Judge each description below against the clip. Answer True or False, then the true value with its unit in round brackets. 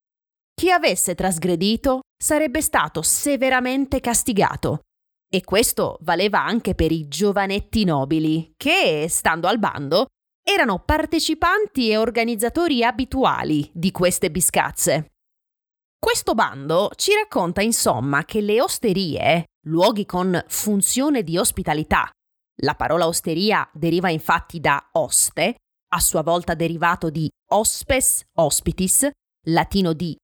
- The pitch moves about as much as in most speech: False (7.5 semitones)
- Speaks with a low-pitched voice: False (205 Hz)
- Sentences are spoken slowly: True (110 wpm)